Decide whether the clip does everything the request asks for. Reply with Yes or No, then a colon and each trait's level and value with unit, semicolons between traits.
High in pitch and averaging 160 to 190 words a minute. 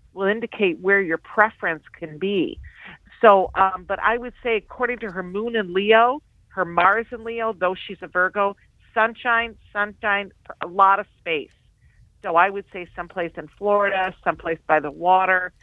Yes: high, 200 Hz; average, 170 wpm